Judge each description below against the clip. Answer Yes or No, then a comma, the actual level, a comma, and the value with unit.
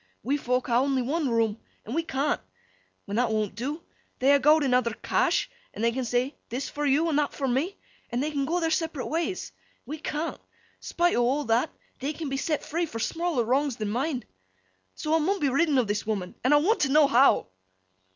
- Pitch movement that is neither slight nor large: Yes, average, 4.1 semitones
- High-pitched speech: Yes, very high, 275 Hz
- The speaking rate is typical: No, fast, 220 wpm